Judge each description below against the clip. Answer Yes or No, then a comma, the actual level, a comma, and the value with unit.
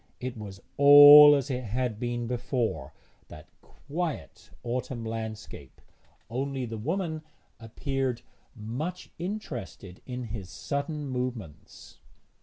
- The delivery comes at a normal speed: No, slow, 105 wpm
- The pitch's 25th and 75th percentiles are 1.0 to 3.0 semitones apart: No, average, 4.1 semitones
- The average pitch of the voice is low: Yes, low, 125 Hz